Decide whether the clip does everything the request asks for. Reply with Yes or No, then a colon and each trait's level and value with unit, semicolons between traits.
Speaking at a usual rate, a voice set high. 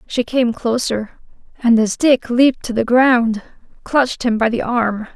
Yes: average, 175 wpm; high, 235 Hz